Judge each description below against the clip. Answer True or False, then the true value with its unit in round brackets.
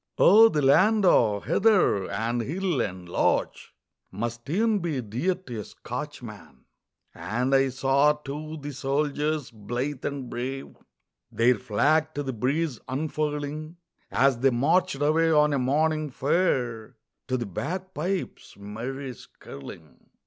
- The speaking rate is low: True (130 wpm)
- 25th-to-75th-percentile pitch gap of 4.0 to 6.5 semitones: True (4.5 semitones)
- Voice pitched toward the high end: False (140 Hz)